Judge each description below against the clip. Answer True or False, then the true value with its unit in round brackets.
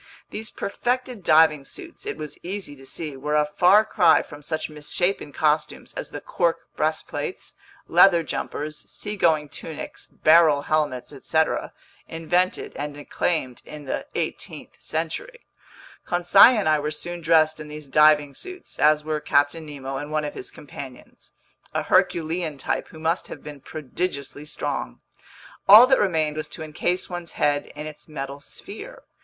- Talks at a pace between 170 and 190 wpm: False (150 wpm)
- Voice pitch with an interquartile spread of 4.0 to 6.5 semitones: False (3.0 semitones)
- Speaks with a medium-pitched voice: True (155 Hz)